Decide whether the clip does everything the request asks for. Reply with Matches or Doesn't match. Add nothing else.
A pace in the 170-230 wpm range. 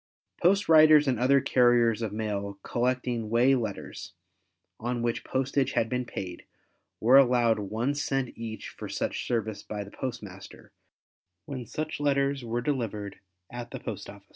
Doesn't match